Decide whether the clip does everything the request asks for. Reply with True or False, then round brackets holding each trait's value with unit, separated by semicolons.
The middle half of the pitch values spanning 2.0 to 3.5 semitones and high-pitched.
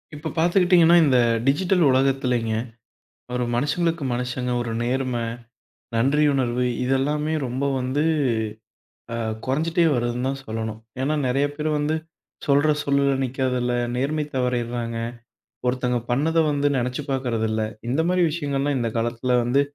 False (3.2 semitones; 135 Hz)